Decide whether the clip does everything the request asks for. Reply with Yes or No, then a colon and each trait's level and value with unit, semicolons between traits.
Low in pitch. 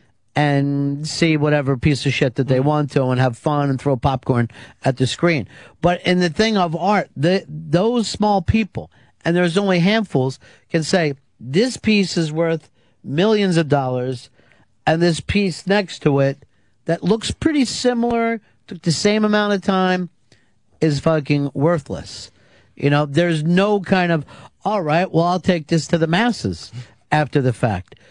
No: medium, 155 Hz